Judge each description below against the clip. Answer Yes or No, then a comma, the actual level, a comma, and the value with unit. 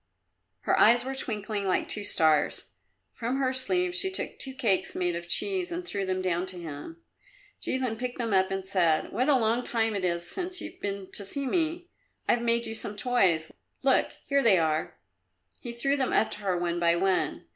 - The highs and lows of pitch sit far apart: Yes, wide, 6.1 semitones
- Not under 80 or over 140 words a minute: No, average, 200 wpm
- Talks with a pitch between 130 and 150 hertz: No, high, 220 Hz